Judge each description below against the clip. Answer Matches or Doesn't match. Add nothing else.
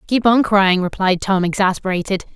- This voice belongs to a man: Doesn't match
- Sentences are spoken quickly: Doesn't match